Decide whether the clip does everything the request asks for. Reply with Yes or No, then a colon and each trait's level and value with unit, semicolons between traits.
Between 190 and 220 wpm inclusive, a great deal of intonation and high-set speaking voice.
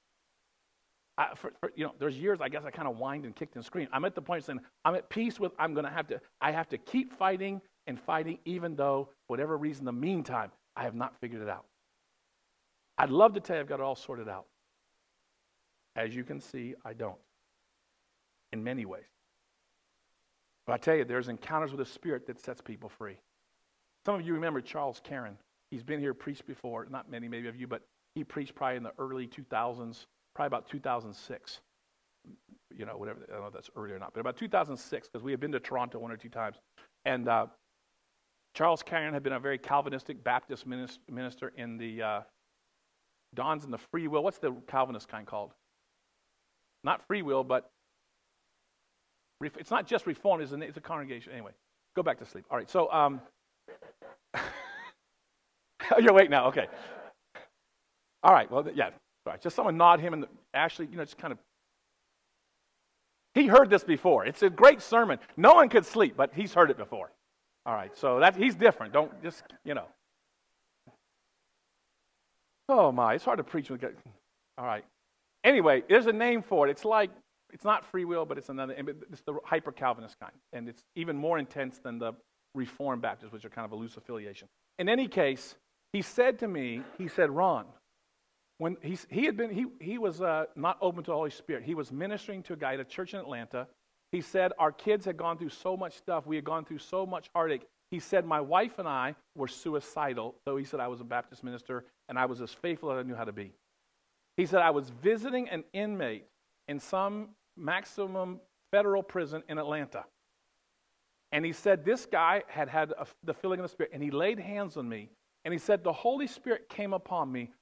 No: fast, 205 wpm; wide, 6.6 semitones; medium, 155 Hz